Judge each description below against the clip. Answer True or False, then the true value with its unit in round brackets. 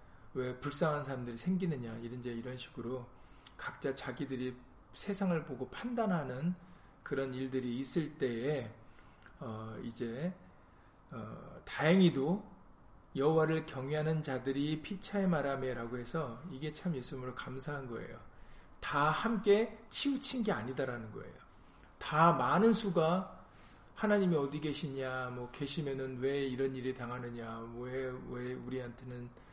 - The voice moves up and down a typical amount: True (4.8 semitones)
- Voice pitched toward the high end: False (135 Hz)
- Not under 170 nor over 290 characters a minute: True (280 characters per minute)